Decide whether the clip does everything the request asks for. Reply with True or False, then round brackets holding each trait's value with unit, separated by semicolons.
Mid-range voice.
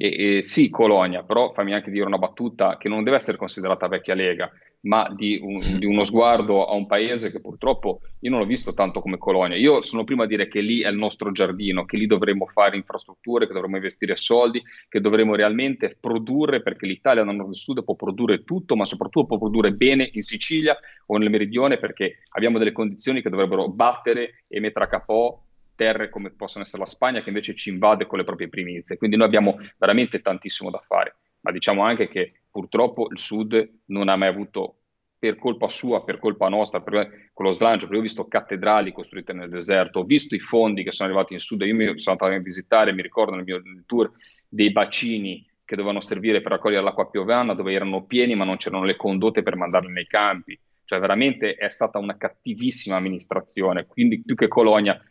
False (105 Hz)